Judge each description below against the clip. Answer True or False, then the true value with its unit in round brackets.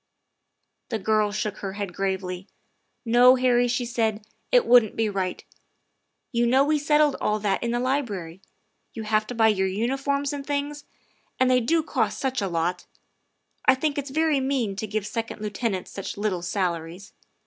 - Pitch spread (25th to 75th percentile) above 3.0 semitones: True (4.9 semitones)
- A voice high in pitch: True (225 Hz)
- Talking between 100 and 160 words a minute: False (180 wpm)